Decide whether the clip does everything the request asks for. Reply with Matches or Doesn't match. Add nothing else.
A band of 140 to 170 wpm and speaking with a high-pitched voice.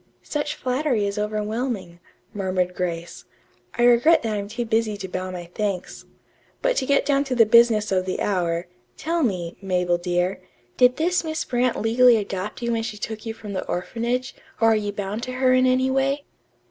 Doesn't match